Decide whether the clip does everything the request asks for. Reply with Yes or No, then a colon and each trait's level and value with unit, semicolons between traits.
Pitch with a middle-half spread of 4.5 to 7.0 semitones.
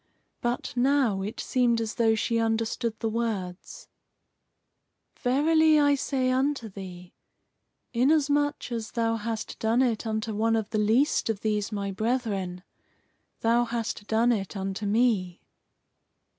No: average, 2.9 semitones